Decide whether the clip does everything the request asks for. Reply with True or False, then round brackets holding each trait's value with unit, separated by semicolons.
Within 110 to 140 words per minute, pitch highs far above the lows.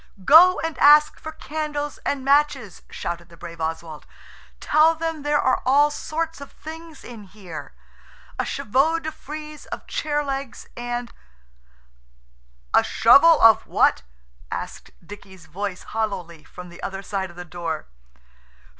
True (135 wpm; 8.9 semitones)